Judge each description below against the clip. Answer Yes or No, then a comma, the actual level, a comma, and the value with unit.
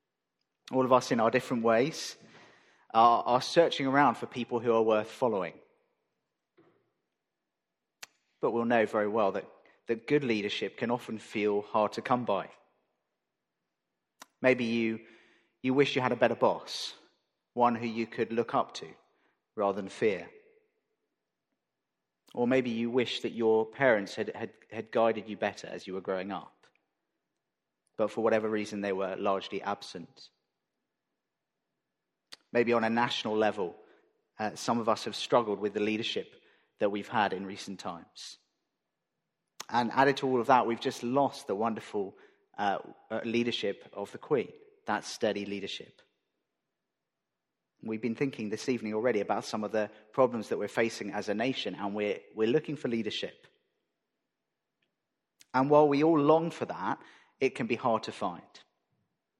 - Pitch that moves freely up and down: No, average, 3.4 semitones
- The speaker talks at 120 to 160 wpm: Yes, average, 155 wpm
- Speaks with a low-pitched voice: Yes, low, 115 Hz